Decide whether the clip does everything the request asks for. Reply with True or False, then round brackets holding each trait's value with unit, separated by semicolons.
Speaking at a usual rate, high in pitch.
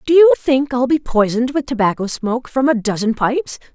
False (210 wpm; 255 Hz)